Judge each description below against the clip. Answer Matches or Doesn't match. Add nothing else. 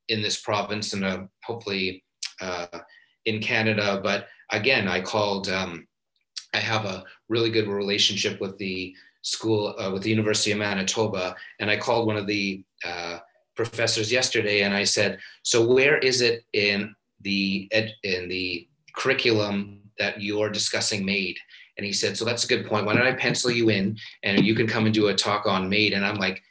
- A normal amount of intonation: Doesn't match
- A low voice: Matches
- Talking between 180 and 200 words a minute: Matches